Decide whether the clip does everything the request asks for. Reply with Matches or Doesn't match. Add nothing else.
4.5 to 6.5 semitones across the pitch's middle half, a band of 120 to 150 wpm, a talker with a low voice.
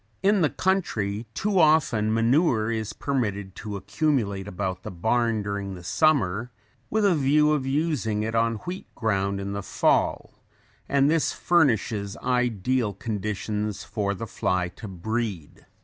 Matches